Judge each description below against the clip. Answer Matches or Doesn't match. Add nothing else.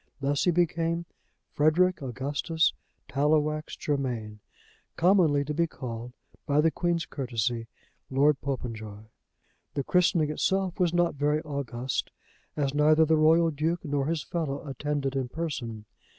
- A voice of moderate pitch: Matches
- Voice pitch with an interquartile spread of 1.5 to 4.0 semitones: Matches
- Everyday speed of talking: Doesn't match